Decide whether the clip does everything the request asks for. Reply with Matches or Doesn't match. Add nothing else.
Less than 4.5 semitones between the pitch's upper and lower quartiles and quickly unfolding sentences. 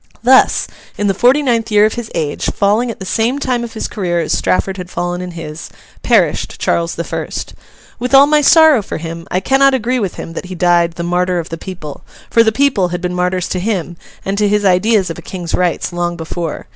Doesn't match